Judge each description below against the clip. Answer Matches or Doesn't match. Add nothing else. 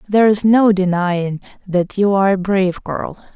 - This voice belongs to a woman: Matches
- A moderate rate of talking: Matches